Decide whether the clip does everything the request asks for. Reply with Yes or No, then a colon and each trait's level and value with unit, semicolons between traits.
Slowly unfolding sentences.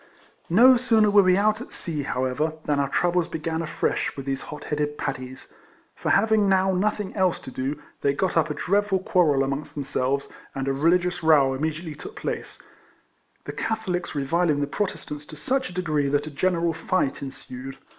No: average, 185 wpm